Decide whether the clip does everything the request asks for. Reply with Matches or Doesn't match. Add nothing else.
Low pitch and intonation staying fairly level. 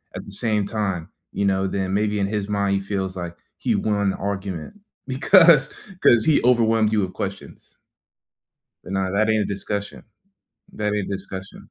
Matches